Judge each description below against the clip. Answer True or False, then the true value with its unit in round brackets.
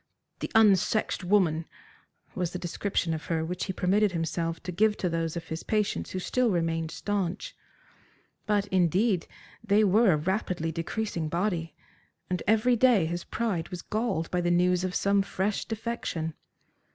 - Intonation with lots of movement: False (3.9 semitones)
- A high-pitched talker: False (180 Hz)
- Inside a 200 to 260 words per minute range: False (160 wpm)